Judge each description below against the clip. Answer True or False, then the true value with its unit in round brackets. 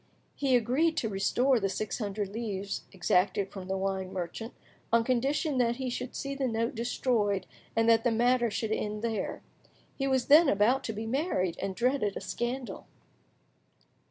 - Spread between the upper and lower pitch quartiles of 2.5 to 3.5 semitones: False (4.1 semitones)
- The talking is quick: False (170 wpm)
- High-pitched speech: True (230 Hz)